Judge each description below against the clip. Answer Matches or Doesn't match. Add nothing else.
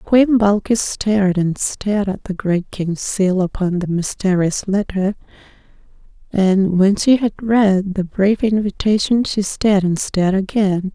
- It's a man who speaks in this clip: Doesn't match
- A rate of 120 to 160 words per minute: Matches